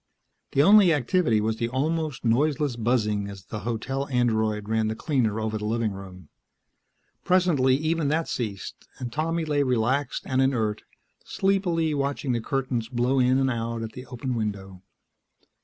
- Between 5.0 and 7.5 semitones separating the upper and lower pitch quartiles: No, average, 4.5 semitones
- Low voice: Yes, low, 125 Hz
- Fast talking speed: No, average, 155 wpm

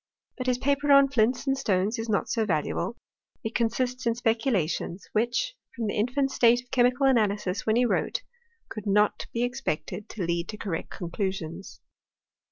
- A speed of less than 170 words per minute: No, average, 175 wpm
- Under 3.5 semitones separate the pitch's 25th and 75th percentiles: No, average, 3.8 semitones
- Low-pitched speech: No, high, 230 Hz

